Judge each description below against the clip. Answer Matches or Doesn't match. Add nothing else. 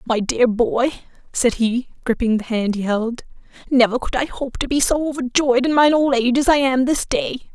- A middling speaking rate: Doesn't match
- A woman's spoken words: Matches